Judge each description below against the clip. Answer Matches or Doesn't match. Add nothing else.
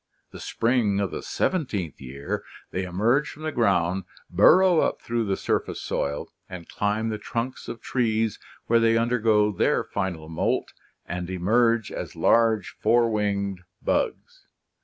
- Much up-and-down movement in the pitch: Doesn't match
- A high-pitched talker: Doesn't match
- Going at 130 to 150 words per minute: Matches